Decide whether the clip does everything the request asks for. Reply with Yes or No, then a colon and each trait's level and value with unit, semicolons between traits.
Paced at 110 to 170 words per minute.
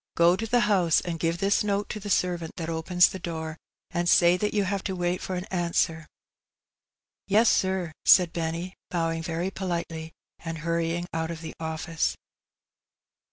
No: average, 180 wpm